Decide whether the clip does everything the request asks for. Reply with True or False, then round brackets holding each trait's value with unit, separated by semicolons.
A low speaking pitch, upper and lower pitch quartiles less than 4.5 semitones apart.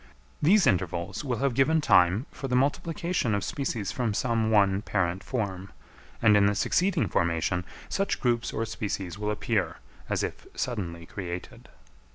False (105 Hz; 5.5 semitones)